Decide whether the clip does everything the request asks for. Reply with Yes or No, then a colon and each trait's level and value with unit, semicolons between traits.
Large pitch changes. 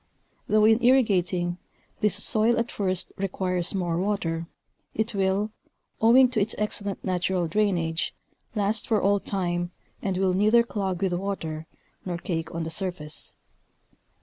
No: average, 3.3 semitones